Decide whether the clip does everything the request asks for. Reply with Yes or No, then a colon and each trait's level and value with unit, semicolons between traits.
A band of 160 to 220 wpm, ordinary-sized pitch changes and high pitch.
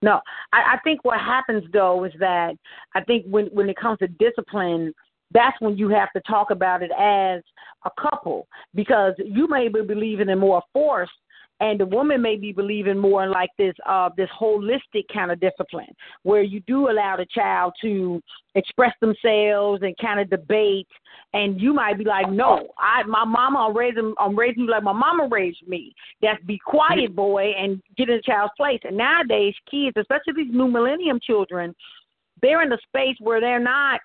Yes: average, 195 wpm; average, 3.9 semitones; high, 215 Hz